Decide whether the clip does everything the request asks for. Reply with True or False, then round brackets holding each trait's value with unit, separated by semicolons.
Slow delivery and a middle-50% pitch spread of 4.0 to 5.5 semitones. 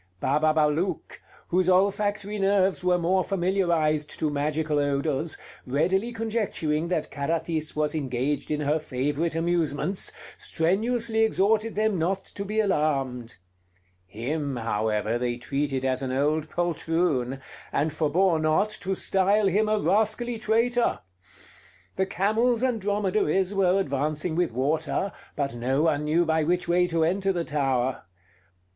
True (130 wpm; 5.0 semitones)